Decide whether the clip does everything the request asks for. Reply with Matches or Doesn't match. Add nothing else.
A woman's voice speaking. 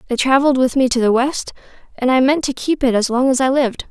Matches